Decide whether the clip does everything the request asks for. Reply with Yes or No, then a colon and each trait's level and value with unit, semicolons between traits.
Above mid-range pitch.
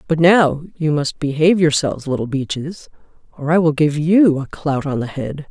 No: medium, 155 Hz